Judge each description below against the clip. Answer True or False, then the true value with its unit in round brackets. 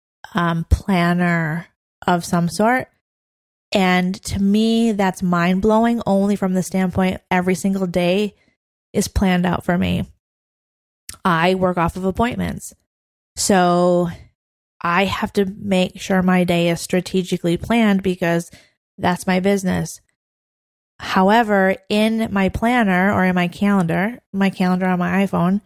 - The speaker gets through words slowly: True (130 wpm)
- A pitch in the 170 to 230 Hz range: True (185 Hz)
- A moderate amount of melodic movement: False (2.1 semitones)